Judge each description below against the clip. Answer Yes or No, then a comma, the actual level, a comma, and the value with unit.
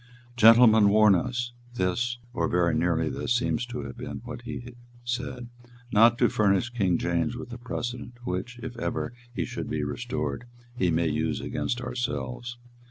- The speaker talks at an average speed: Yes, average, 165 wpm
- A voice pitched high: No, low, 120 Hz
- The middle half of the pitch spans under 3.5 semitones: No, average, 5.0 semitones